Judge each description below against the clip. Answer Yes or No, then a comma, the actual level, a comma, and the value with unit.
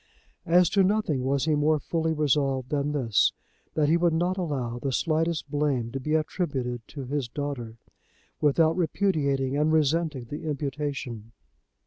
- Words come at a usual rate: Yes, average, 150 wpm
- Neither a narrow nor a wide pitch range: Yes, average, 3.2 semitones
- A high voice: No, medium, 145 Hz